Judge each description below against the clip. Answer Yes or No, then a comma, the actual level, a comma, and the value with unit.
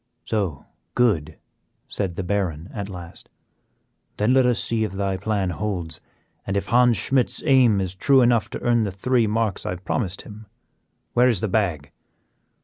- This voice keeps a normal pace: Yes, average, 175 wpm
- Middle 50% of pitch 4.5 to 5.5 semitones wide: No, average, 4.1 semitones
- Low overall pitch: Yes, low, 105 Hz